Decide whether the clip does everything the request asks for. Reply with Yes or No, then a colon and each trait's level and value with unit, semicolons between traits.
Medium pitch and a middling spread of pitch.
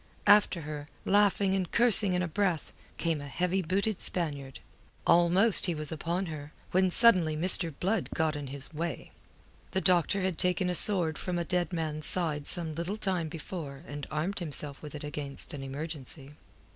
Yes: medium, 170 Hz; average, 3.7 semitones